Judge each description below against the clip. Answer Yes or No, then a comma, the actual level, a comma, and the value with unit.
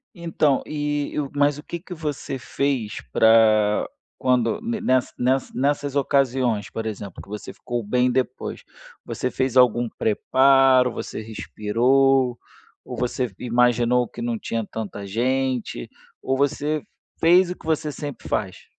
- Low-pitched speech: Yes, low, 130 Hz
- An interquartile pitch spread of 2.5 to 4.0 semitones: Yes, average, 3.6 semitones